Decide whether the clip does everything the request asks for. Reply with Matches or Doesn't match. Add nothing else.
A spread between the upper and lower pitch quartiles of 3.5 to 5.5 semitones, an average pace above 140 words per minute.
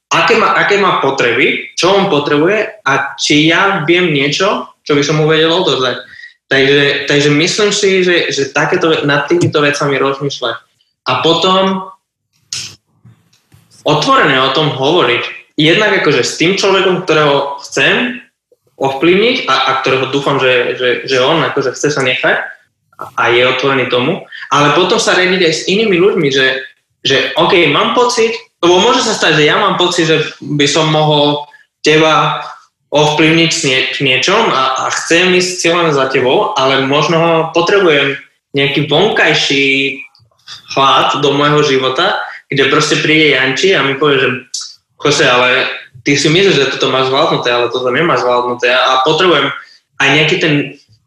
Matches